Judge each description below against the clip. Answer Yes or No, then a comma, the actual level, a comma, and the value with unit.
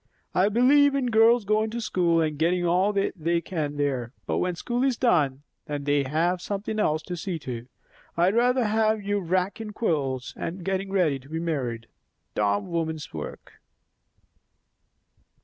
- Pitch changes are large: Yes, wide, 6.2 semitones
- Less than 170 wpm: Yes, average, 160 wpm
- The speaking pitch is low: No, medium, 175 Hz